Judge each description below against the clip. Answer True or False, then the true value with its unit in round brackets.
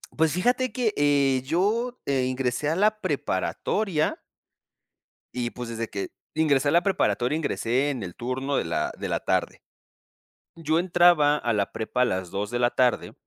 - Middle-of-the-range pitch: True (145 Hz)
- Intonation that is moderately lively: False (5.9 semitones)